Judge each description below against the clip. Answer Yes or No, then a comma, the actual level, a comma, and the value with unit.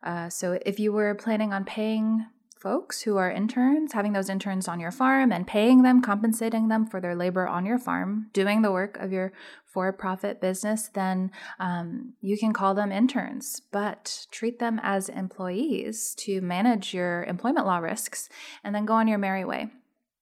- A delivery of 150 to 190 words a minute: Yes, average, 185 wpm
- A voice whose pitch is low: No, high, 210 Hz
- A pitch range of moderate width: Yes, average, 3.4 semitones